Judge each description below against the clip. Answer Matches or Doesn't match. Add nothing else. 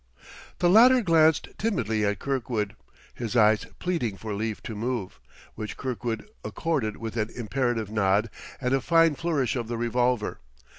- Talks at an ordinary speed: Matches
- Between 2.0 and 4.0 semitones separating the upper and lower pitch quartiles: Doesn't match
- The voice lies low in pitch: Matches